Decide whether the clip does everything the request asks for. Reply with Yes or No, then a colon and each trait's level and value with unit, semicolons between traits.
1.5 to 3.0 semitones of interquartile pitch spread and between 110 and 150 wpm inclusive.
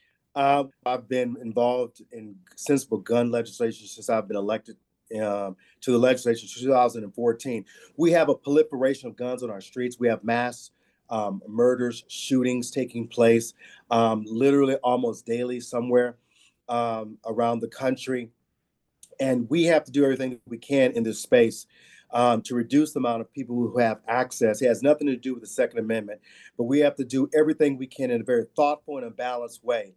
No: narrow, 2.5 semitones; average, 180 wpm